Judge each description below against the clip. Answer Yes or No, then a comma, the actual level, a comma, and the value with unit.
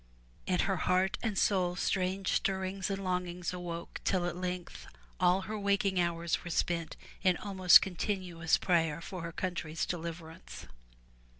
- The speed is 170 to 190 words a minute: No, average, 145 wpm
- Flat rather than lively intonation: Yes, narrow, 1.9 semitones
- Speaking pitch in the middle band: Yes, medium, 180 Hz